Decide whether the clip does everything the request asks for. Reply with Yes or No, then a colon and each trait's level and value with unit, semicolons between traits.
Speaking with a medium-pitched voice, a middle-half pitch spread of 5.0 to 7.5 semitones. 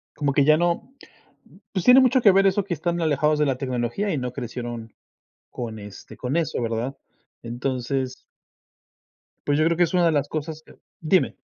Yes: medium, 145 Hz; wide, 5.5 semitones